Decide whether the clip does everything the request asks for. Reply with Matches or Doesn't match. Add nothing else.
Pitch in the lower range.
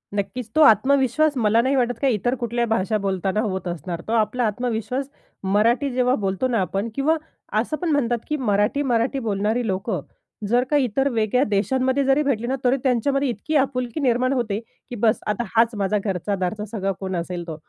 Doesn't match